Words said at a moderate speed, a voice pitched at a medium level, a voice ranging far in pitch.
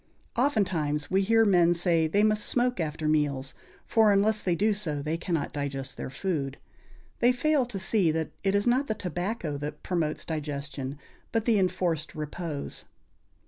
Yes: average, 165 wpm; medium, 175 Hz; wide, 5.8 semitones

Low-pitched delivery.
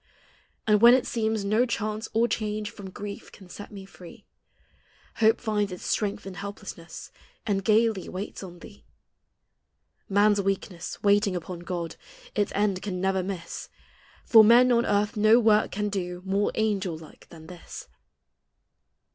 No: high, 205 Hz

